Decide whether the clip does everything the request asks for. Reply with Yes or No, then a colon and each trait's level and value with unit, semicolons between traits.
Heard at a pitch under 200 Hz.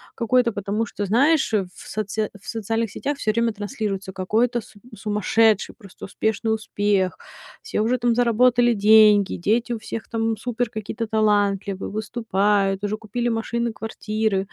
No: high, 220 Hz